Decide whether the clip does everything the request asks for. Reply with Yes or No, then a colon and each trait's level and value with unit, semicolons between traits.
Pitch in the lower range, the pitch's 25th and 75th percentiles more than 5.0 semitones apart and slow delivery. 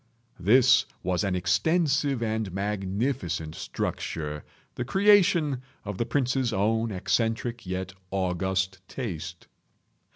Yes: low, 105 Hz; wide, 5.4 semitones; slow, 100 wpm